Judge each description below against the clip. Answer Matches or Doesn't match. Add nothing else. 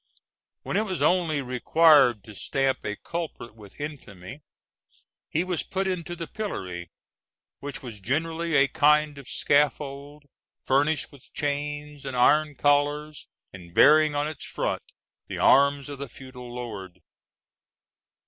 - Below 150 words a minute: Matches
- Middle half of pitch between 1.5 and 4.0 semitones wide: Matches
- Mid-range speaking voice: Matches